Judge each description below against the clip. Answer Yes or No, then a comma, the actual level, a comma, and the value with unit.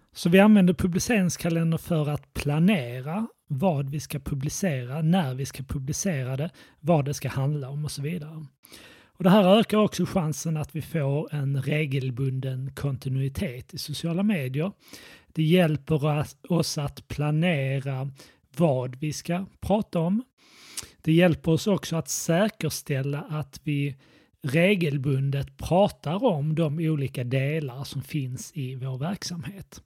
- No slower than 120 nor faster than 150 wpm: Yes, average, 135 wpm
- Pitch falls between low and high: Yes, medium, 150 Hz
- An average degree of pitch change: Yes, average, 3.8 semitones